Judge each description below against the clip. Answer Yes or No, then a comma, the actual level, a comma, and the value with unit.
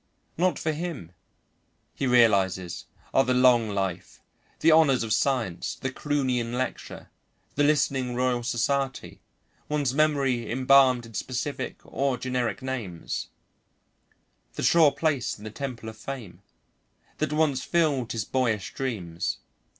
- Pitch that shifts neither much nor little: Yes, average, 3.3 semitones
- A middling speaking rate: No, slow, 125 wpm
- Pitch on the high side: No, low, 130 Hz